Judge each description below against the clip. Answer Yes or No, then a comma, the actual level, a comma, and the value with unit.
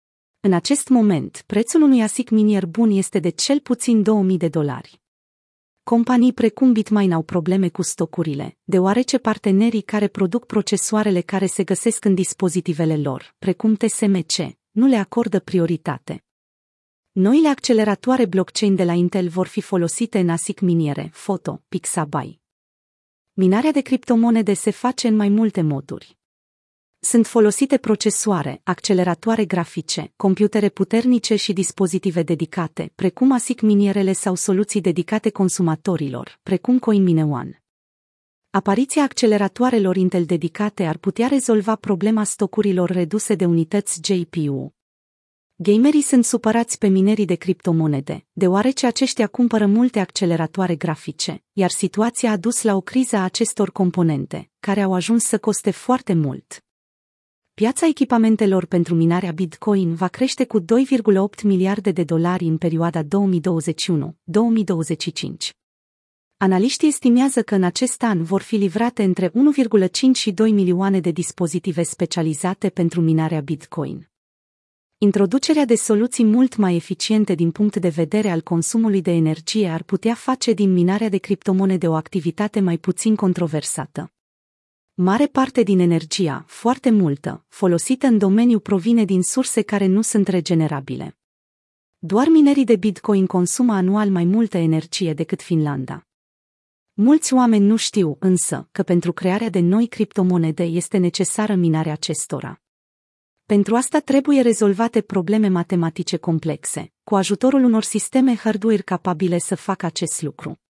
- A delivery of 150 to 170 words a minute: No, average, 135 wpm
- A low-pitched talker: No, high, 195 Hz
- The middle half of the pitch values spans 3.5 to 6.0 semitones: Yes, average, 4.1 semitones